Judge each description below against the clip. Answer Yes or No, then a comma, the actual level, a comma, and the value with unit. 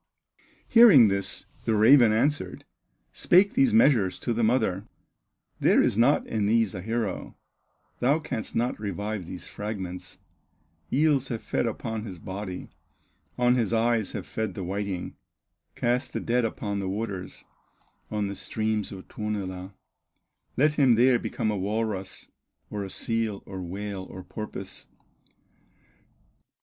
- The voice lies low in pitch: Yes, low, 110 Hz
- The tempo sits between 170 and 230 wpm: No, slow, 135 wpm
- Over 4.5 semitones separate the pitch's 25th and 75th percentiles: No, average, 3.5 semitones